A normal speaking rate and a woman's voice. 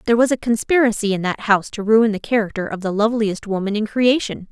No: fast, 225 wpm; female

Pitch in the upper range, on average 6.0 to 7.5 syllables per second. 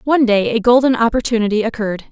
Yes: high, 230 Hz; 7.1 syllables/s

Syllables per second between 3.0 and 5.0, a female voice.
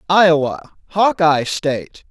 No: 4.6 syllables/s; male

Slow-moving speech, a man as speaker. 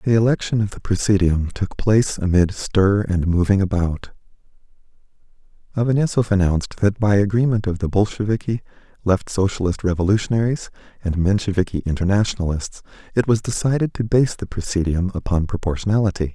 Yes: slow, 130 wpm; male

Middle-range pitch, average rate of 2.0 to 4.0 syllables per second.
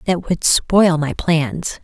Yes: medium, 170 Hz; 3.0 syllables/s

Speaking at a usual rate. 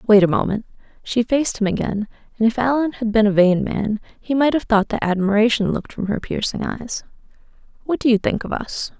No: fast, 215 wpm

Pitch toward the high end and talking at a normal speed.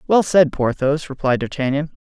No: medium, 145 Hz; average, 145 wpm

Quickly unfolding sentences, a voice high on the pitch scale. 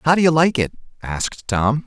No: fast, 225 wpm; low, 135 Hz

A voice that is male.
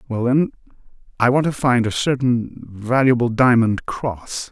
Yes: male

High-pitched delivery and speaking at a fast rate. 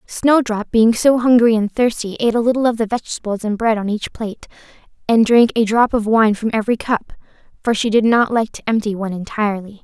Yes: high, 220 Hz; fast, 215 wpm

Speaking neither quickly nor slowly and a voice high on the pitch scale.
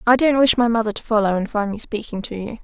No: fast, 295 wpm; high, 220 Hz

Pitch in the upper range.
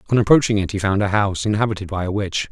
No: low, 100 Hz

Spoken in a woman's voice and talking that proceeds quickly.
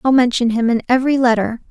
Yes: female; fast, 210 wpm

